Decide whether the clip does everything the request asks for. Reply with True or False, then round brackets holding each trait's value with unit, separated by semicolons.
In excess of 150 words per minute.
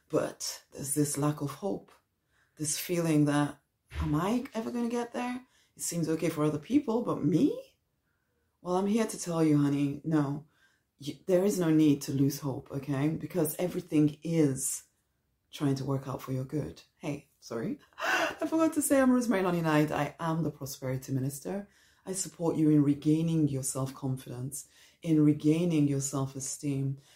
True (170 wpm)